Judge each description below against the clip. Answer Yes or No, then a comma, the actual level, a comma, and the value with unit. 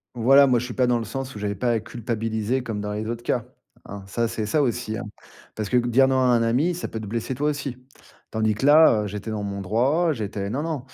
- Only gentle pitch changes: No, average, 3.5 semitones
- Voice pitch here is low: Yes, low, 120 Hz